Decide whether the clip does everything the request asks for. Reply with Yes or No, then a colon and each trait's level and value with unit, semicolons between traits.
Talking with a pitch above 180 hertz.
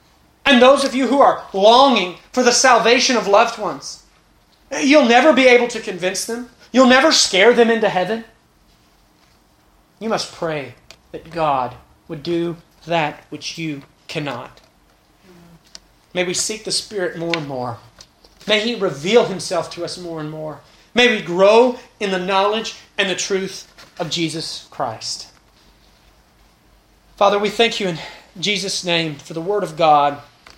Yes: high, 190 Hz